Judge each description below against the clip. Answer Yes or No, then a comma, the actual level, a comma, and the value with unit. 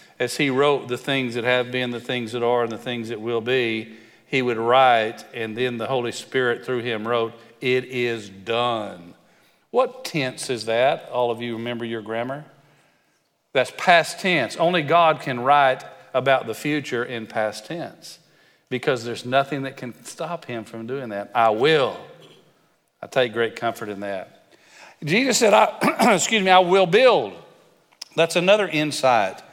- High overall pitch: No, low, 125 Hz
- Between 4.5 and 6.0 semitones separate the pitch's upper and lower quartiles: No, average, 4.0 semitones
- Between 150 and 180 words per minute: Yes, average, 170 wpm